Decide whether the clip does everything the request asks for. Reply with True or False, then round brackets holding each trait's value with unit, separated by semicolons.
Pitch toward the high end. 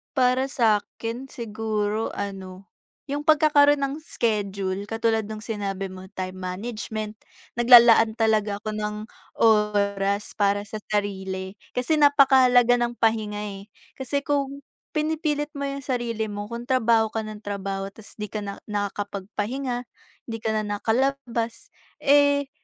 True (220 Hz)